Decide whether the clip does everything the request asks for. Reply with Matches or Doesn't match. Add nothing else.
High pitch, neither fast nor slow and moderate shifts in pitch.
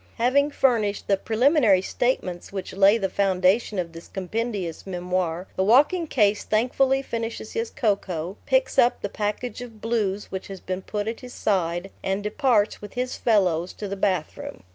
Matches